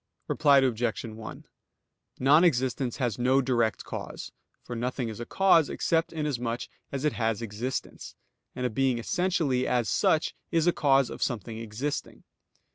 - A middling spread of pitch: Yes, average, 3.8 semitones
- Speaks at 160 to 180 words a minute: No, average, 150 wpm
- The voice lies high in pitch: No, low, 125 Hz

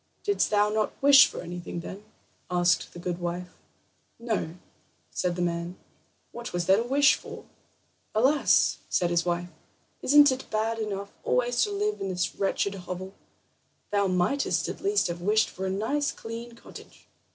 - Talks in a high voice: Yes, high, 200 Hz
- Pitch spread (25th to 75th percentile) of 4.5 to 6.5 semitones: Yes, average, 5.2 semitones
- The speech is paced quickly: No, average, 165 wpm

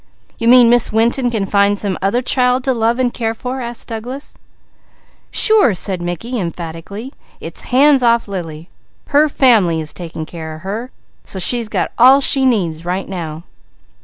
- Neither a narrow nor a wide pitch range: No, wide, 5.8 semitones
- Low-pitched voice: No, high, 225 Hz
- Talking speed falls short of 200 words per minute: Yes, average, 165 wpm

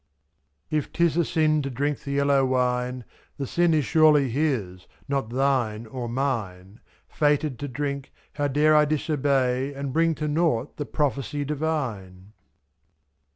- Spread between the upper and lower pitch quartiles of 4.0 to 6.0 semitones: No, average, 3.3 semitones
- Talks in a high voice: No, medium, 140 Hz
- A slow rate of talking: No, average, 155 wpm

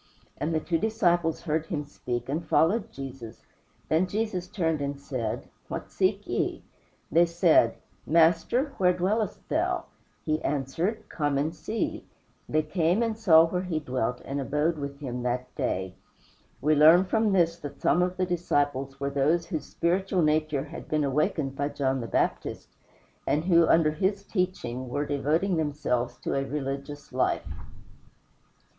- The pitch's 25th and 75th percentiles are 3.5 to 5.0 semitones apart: Yes, average, 4.2 semitones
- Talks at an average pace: Yes, average, 155 wpm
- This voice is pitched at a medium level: Yes, medium, 155 Hz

